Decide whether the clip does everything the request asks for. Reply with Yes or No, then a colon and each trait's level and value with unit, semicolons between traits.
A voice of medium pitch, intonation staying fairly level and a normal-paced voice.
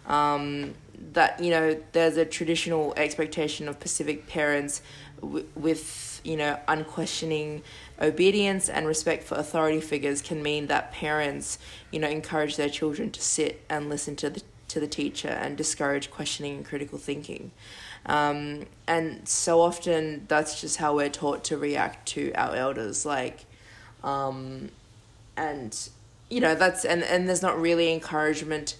Yes: medium, 150 Hz; narrow, 1.9 semitones; average, 160 wpm